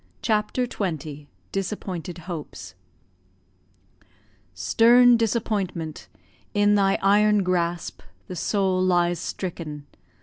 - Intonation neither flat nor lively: Yes, average, 3.8 semitones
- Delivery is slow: Yes, slow, 80 wpm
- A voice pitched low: No, medium, 185 Hz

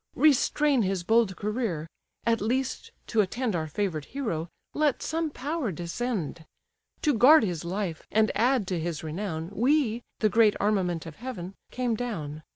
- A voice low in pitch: No, high, 215 Hz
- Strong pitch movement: Yes, wide, 6.4 semitones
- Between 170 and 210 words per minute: No, average, 155 wpm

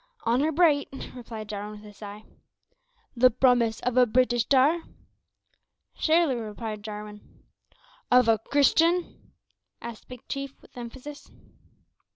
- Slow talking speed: Yes, slow, 120 wpm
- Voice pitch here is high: Yes, high, 245 Hz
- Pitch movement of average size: Yes, average, 4.2 semitones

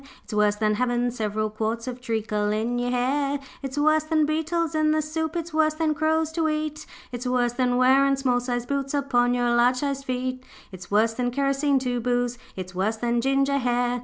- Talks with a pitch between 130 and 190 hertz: No, very high, 250 Hz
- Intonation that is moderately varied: Yes, average, 3.4 semitones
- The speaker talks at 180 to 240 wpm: Yes, average, 200 wpm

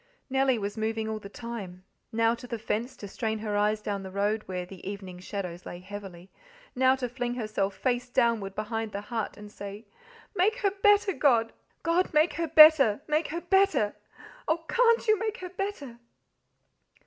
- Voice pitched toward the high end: Yes, high, 225 Hz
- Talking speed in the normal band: Yes, average, 180 wpm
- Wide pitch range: Yes, wide, 6.9 semitones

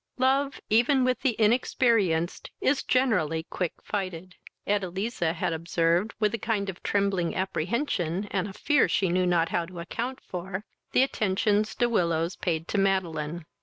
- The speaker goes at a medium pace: Yes, average, 155 wpm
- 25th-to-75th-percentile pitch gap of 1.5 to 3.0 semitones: No, average, 4.9 semitones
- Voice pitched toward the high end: Yes, high, 195 Hz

